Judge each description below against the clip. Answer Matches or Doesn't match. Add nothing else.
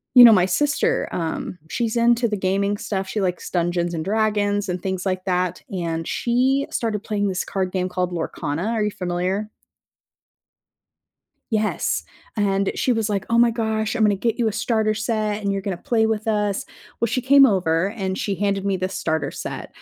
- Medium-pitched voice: Doesn't match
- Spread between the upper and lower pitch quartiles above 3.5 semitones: Doesn't match